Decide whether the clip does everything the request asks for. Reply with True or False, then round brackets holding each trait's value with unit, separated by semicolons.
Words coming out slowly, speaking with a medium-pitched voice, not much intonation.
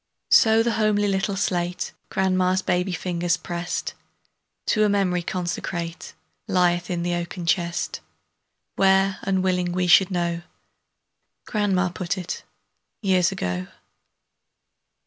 True (110 wpm; 180 Hz; 1.8 semitones)